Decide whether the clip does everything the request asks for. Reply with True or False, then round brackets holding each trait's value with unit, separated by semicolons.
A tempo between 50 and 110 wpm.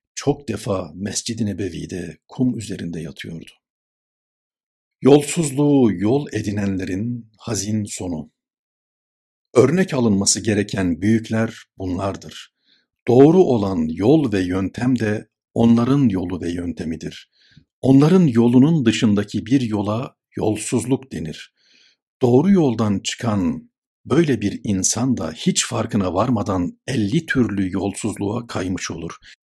True (100 wpm)